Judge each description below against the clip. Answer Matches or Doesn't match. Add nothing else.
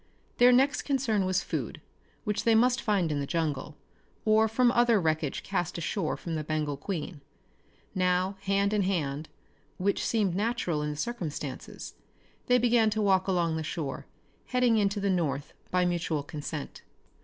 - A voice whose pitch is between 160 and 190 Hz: Matches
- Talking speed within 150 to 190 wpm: Matches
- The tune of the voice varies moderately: Doesn't match